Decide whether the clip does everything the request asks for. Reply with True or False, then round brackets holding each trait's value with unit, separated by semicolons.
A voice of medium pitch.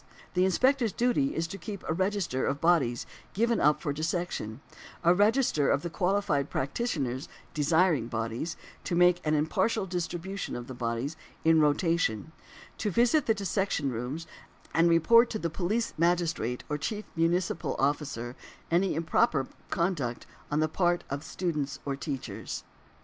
True (165 Hz)